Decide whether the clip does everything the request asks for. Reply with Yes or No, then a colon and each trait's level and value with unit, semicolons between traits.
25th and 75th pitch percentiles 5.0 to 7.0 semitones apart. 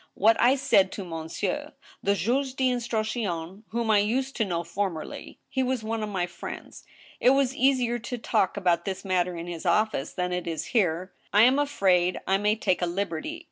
Yes: wide, 5.4 semitones